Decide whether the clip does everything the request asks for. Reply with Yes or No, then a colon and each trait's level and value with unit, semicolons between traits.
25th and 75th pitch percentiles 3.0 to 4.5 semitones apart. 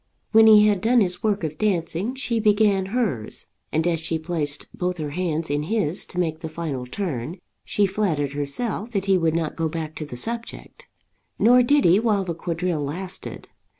No: average, 4.9 semitones